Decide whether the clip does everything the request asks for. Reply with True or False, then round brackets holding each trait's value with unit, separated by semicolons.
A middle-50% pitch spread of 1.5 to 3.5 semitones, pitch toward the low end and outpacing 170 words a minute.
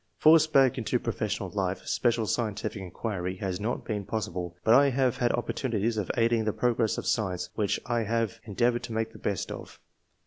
True (2.8 semitones; 115 Hz; 200 wpm)